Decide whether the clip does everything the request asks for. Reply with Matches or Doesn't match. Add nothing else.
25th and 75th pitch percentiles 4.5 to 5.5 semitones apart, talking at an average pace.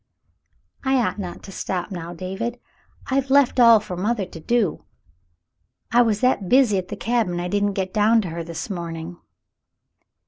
Matches